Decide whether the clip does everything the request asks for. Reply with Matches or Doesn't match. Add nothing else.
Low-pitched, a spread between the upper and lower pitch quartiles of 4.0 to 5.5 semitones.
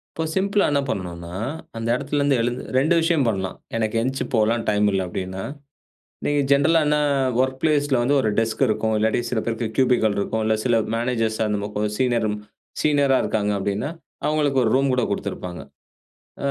Matches